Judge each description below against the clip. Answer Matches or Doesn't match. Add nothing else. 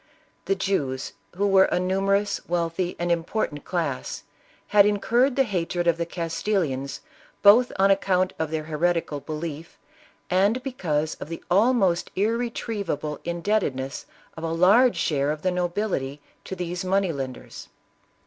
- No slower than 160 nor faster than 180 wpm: Doesn't match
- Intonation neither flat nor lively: Matches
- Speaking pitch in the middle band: Matches